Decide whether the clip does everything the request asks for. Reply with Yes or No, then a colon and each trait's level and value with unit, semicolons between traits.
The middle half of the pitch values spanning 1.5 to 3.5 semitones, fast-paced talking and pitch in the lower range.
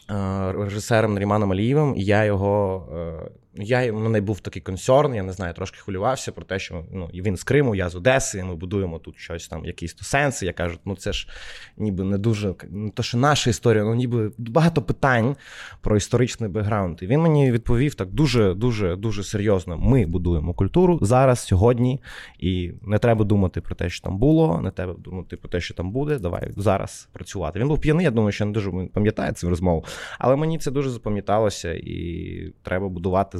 No: average, 4.7 semitones; fast, 200 wpm; low, 100 Hz